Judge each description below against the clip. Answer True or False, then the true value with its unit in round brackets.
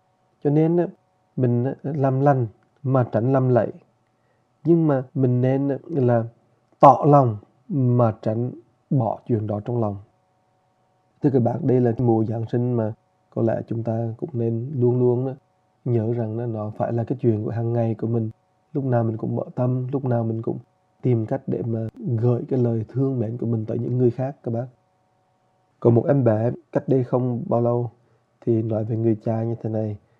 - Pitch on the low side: True (120 Hz)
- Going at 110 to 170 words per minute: False (190 wpm)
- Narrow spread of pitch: True (2.3 semitones)